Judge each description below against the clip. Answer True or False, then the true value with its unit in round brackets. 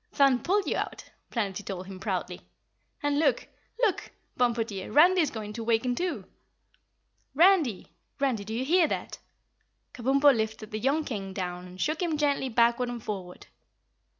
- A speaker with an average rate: True (160 wpm)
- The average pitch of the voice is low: False (240 Hz)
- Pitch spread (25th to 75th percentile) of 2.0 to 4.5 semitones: False (5.6 semitones)